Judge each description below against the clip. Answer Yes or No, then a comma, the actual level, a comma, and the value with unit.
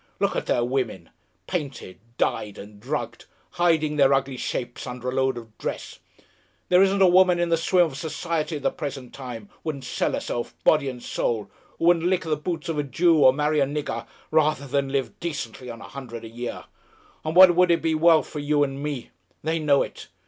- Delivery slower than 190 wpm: No, fast, 205 wpm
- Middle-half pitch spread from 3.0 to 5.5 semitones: Yes, average, 4.6 semitones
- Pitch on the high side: No, medium, 145 Hz